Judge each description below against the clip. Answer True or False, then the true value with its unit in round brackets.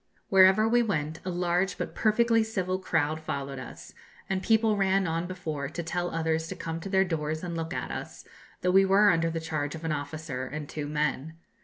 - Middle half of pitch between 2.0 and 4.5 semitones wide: True (3.5 semitones)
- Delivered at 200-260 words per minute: True (205 wpm)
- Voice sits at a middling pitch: True (165 Hz)